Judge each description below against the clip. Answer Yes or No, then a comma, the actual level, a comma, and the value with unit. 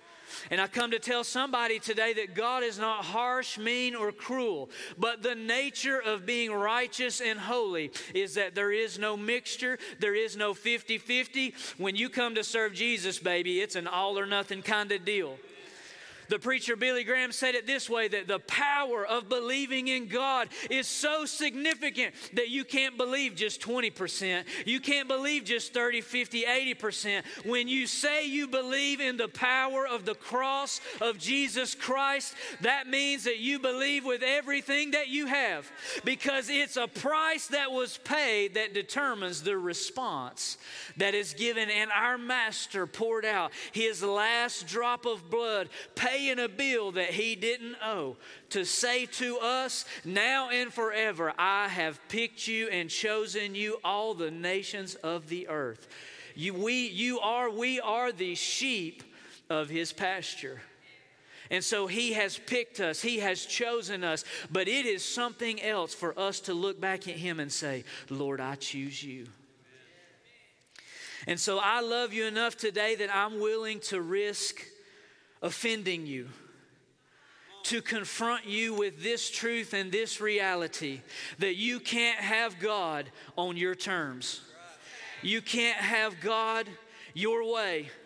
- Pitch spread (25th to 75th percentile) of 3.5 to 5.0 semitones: Yes, average, 4.2 semitones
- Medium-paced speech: Yes, average, 155 wpm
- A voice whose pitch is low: No, high, 225 Hz